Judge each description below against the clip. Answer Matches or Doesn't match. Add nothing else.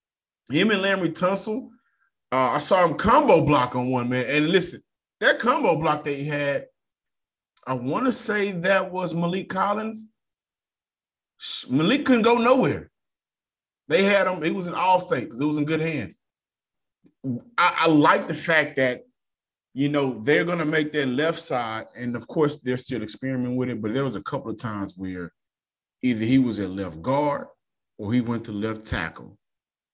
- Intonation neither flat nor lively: Doesn't match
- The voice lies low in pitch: Doesn't match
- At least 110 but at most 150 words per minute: Doesn't match